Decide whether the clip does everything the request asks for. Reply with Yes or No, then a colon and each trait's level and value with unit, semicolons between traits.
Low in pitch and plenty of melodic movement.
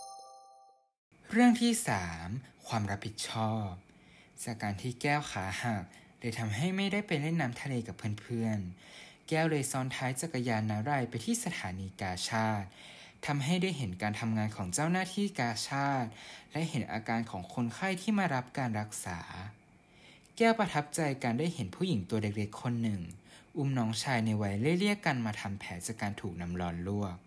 Yes: low, 120 Hz; wide, 5.8 semitones